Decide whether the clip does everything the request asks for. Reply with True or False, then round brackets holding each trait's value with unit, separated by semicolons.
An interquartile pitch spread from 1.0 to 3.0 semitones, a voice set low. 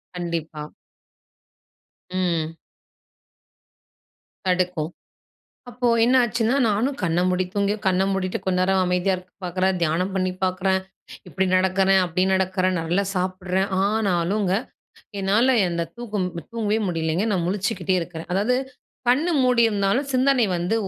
False (2.5 semitones; 190 Hz)